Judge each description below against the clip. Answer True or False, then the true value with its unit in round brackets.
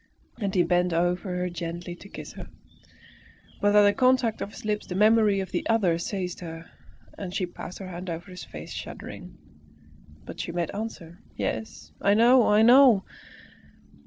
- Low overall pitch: False (185 Hz)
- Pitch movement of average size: True (3.3 semitones)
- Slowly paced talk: False (175 wpm)